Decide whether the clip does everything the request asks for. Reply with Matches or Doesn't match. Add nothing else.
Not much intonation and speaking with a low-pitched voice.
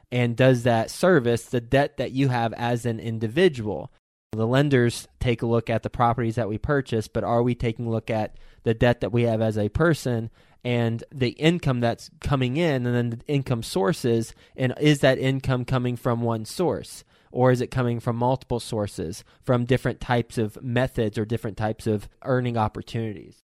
Matches